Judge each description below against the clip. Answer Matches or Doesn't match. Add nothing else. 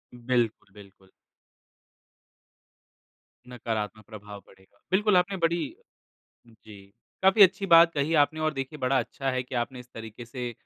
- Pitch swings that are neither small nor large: Doesn't match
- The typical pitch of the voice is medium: Doesn't match